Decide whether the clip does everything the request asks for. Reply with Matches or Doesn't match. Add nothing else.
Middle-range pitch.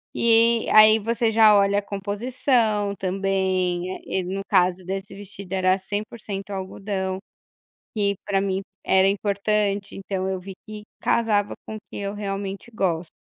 Doesn't match